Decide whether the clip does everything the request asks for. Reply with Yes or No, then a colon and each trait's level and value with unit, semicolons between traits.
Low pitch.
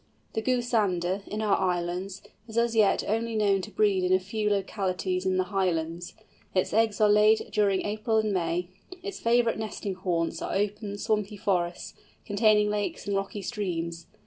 No: high, 200 Hz